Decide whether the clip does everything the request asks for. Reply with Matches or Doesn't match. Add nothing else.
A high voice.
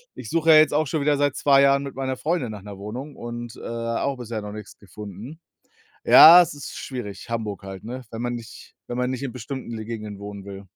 Doesn't match